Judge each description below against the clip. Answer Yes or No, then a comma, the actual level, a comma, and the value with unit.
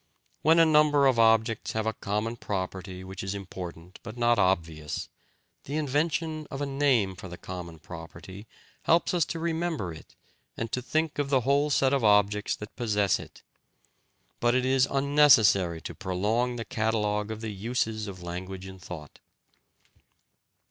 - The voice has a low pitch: Yes, low, 110 Hz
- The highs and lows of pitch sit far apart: Yes, wide, 6.4 semitones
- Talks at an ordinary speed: Yes, average, 160 wpm